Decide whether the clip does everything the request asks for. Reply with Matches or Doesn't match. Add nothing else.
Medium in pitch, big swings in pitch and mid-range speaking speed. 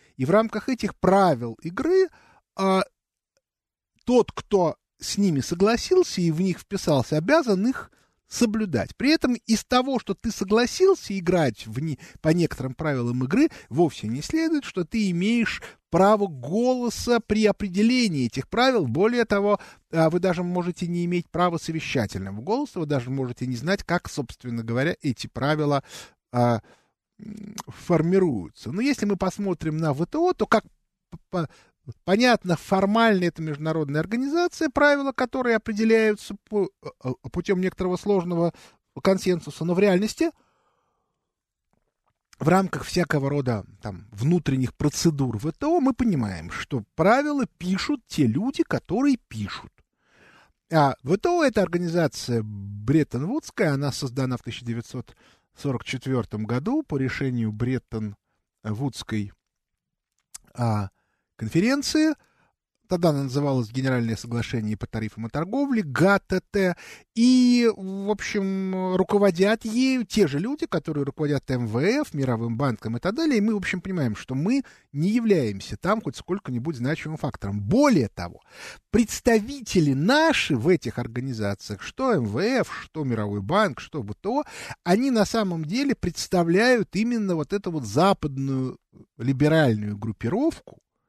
Matches